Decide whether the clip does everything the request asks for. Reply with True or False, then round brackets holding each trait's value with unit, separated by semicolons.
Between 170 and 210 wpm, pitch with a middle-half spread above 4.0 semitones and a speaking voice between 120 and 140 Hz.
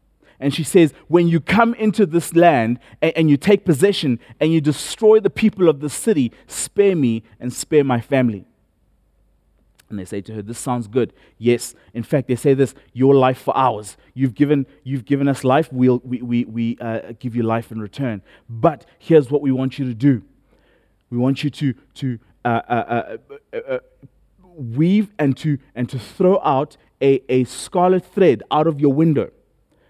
True (190 wpm; 5.2 semitones; 135 Hz)